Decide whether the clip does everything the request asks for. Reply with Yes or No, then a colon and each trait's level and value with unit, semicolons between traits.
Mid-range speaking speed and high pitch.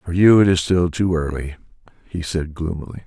No: average, 195 wpm; very low, 85 Hz